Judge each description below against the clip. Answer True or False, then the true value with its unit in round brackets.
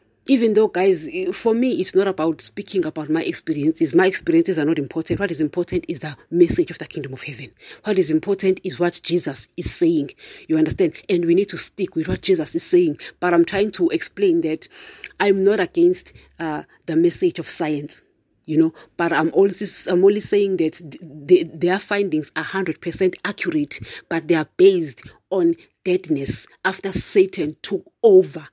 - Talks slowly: False (185 wpm)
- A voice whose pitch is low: False (190 Hz)